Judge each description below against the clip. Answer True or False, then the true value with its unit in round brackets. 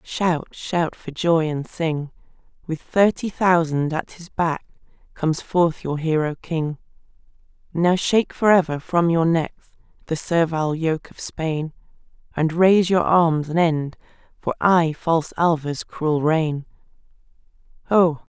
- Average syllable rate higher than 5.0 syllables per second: False (4.0 syllables/s)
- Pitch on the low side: False (165 Hz)